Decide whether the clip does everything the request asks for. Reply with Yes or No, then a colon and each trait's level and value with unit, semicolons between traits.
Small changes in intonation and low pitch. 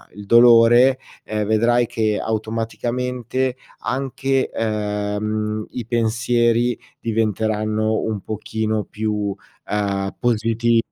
Yes: narrow, 1.9 semitones; low, 110 Hz